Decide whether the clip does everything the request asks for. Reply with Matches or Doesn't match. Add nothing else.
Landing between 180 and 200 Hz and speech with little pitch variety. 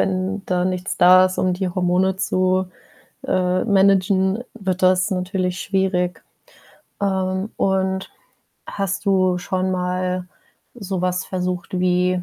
Matches